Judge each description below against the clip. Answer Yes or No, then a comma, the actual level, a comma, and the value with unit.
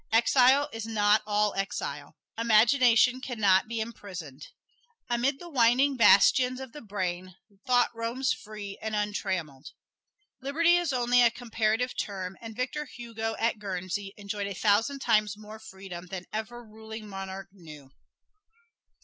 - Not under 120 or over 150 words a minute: Yes, average, 140 wpm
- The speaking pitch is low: No, high, 220 Hz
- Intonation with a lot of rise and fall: No, average, 3.6 semitones